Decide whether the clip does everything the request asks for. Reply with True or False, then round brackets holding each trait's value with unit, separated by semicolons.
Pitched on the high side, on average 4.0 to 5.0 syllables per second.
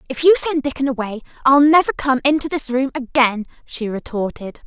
False (265 Hz; 5.5 syllables/s)